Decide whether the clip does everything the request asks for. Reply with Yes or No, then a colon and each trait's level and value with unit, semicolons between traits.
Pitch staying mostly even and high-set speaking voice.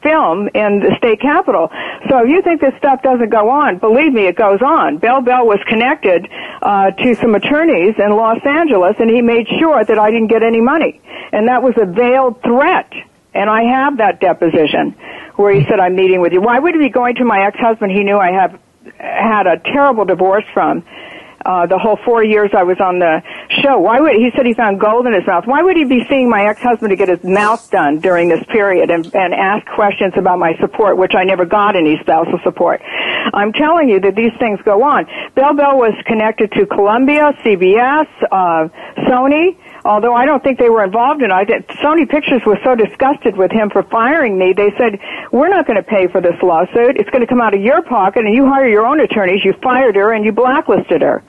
No: average, 4.9 semitones; high, 225 Hz